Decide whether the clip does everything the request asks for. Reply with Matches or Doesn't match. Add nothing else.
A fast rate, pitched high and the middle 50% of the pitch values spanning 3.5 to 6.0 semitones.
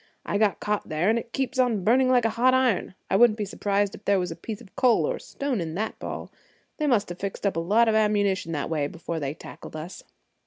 Matches